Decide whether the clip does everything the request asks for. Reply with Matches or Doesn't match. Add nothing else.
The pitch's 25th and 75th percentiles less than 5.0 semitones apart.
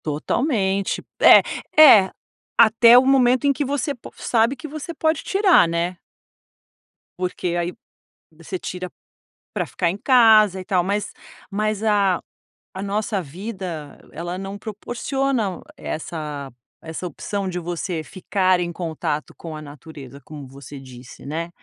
Doesn't match